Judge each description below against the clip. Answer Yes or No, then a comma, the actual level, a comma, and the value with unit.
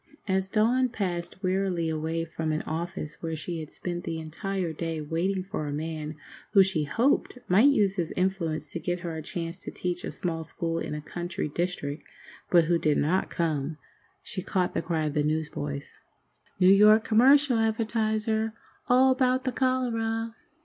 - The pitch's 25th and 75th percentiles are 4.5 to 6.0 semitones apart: Yes, average, 5.2 semitones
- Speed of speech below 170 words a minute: No, average, 175 wpm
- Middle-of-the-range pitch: Yes, medium, 175 Hz